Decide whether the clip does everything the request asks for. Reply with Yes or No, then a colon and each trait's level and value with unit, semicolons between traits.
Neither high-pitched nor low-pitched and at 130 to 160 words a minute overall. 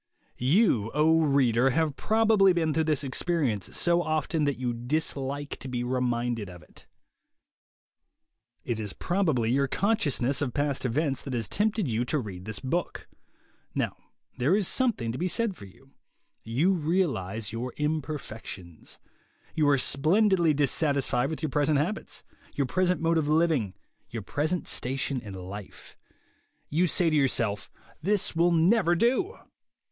Yes: medium, 145 Hz; average, 150 wpm